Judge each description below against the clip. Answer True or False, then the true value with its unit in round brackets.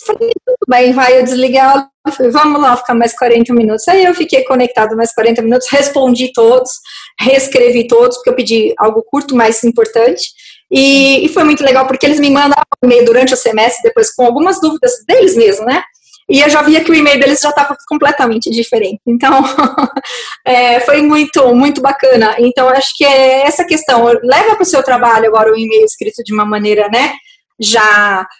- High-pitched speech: True (265 Hz)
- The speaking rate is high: True (190 wpm)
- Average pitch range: True (3.8 semitones)